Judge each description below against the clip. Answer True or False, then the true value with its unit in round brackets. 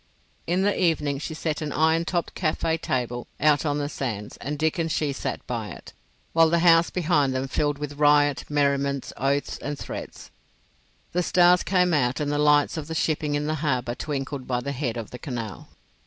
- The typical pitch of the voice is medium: True (145 Hz)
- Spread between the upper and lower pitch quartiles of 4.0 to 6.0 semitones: False (2.8 semitones)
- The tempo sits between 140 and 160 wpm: False (200 wpm)